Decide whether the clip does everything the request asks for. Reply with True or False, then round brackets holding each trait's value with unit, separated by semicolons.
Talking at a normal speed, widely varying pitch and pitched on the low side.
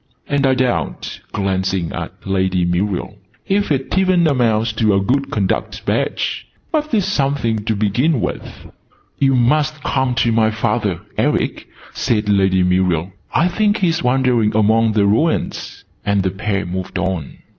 True (150 wpm; 6.0 semitones; 110 Hz)